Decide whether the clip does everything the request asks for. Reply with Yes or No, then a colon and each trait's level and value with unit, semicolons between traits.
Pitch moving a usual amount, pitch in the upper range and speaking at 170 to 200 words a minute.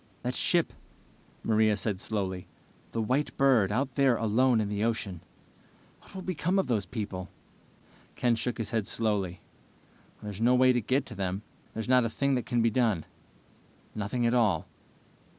No: average, 3.7 semitones; low, 115 Hz; average, 175 wpm